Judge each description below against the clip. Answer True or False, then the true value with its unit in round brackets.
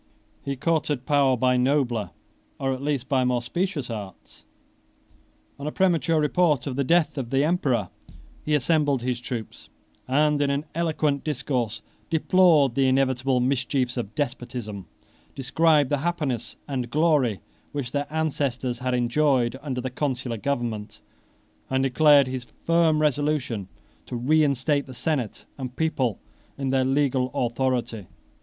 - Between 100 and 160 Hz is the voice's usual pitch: True (135 Hz)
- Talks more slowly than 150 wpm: True (140 wpm)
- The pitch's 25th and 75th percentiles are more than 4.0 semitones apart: False (3.2 semitones)